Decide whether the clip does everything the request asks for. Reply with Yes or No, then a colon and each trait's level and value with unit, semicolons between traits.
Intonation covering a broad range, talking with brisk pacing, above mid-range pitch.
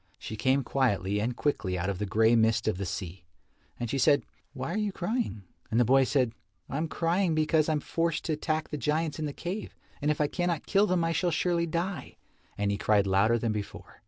No: wide, 7.2 semitones; fast, 230 wpm; medium, 140 Hz